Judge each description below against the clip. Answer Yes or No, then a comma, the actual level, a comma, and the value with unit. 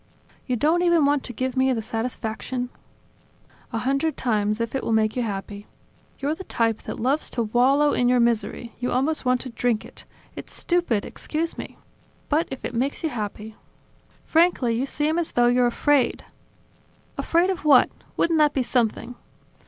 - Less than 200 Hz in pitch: No, very high, 250 Hz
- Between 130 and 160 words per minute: No, average, 185 wpm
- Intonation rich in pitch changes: No, average, 4.3 semitones